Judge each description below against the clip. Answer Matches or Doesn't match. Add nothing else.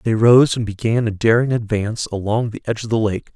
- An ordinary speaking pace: Doesn't match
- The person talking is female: Doesn't match